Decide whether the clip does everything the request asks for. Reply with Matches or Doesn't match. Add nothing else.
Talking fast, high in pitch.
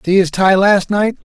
Matches